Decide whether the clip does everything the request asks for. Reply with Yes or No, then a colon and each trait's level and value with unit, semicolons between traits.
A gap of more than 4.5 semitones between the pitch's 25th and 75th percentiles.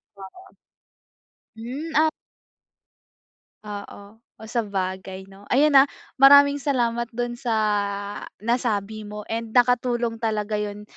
No: average, 3.3 semitones